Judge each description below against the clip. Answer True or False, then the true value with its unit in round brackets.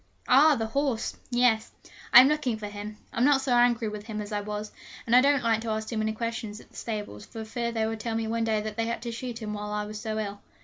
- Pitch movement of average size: False (2.1 semitones)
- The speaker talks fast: True (275 wpm)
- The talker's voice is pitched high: True (225 Hz)